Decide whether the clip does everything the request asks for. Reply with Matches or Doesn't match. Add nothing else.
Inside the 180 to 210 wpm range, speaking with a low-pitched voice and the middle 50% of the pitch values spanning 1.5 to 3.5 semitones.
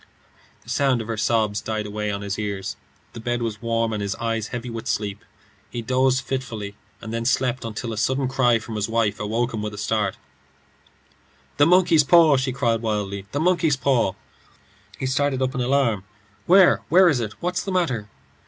Doesn't match